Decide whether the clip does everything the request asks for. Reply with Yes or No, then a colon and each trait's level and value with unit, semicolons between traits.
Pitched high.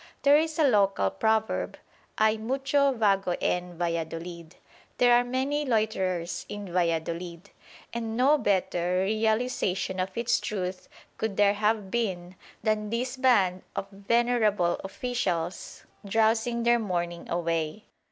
Yes: high, 205 Hz